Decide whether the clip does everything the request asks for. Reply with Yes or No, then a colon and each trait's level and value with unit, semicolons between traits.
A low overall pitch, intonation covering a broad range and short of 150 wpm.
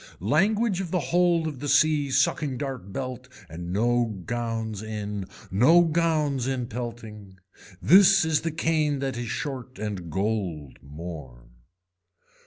Yes: low, 125 Hz; wide, 6.9 semitones; slow, 135 wpm